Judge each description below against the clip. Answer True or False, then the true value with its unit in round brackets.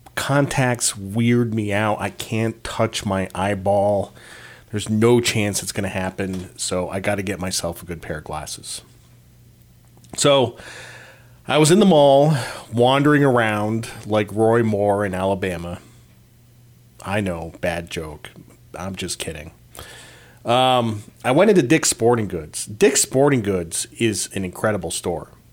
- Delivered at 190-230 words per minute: False (145 wpm)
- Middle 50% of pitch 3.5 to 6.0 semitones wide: True (4.4 semitones)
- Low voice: True (105 Hz)